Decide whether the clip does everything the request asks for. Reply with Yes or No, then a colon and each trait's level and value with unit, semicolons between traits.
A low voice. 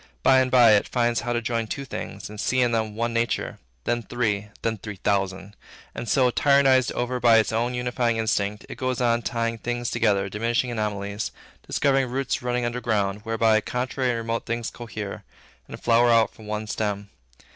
Yes: low, 115 Hz